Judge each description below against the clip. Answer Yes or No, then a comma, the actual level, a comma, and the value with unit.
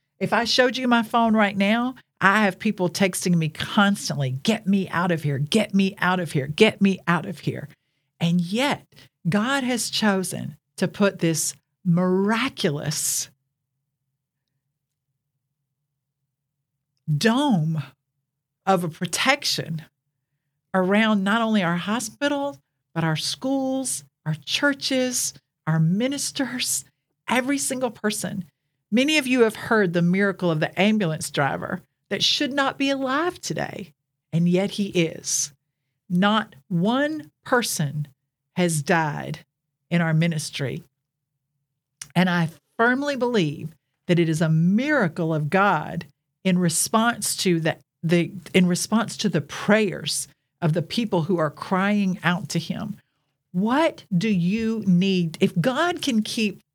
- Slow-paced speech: Yes, slow, 130 wpm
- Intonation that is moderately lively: No, wide, 6.5 semitones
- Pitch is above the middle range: No, medium, 175 Hz